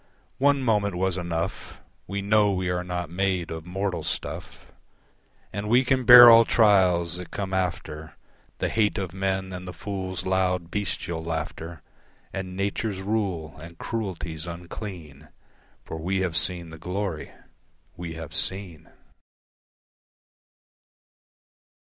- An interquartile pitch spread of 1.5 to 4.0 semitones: Yes, average, 2.9 semitones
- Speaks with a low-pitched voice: Yes, very low, 95 Hz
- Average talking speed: No, slow, 130 wpm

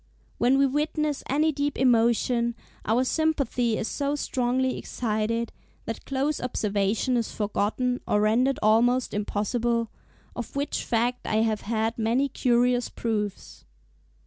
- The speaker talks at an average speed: No, slow, 125 wpm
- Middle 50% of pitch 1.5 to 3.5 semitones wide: Yes, average, 2.9 semitones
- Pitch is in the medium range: No, high, 240 Hz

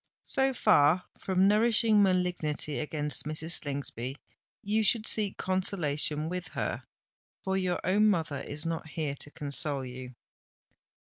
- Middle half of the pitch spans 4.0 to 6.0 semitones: Yes, average, 5.0 semitones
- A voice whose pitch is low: No, medium, 165 Hz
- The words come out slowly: Yes, slow, 130 wpm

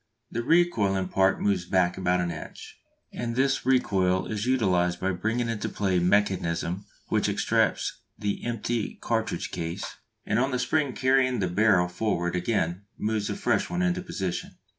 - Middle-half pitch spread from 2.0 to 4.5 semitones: No, average, 5.2 semitones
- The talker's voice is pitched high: No, low, 100 Hz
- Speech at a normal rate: Yes, average, 160 wpm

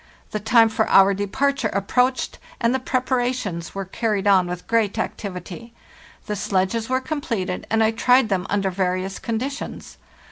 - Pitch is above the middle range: Yes, high, 220 Hz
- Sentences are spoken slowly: No, average, 155 wpm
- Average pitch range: Yes, average, 4.2 semitones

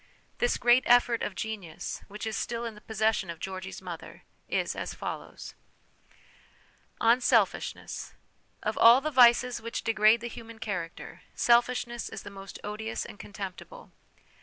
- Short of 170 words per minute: Yes, average, 160 wpm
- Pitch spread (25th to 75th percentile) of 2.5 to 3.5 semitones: Yes, average, 3.0 semitones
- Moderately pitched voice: No, high, 225 Hz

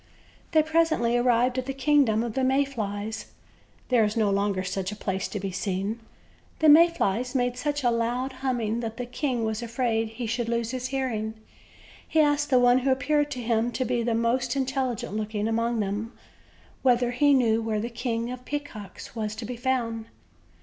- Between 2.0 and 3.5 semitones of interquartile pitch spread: Yes, average, 2.8 semitones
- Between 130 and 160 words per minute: No, average, 195 wpm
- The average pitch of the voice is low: No, high, 240 Hz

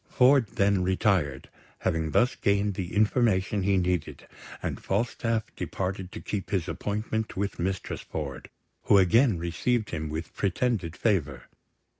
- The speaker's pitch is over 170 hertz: No, very low, 95 Hz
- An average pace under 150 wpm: Yes, slow, 135 wpm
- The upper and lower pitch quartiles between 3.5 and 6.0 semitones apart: Yes, average, 3.8 semitones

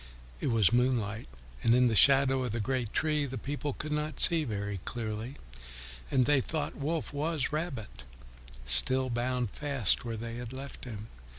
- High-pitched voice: No, low, 125 Hz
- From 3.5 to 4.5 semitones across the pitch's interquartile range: Yes, average, 4.0 semitones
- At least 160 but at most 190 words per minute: Yes, average, 170 wpm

